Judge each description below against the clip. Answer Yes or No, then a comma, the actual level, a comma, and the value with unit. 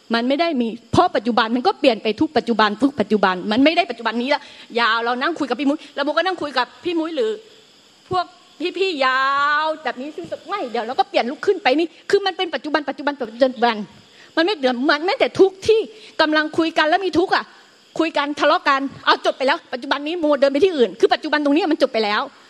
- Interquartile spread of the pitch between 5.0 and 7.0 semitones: Yes, average, 5.3 semitones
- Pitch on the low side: No, very high, 295 Hz